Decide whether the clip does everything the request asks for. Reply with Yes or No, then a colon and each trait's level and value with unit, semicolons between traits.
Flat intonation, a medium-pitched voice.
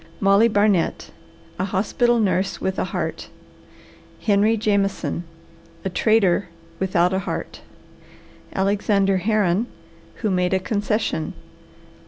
No: narrow, 2.1 semitones; high, 200 Hz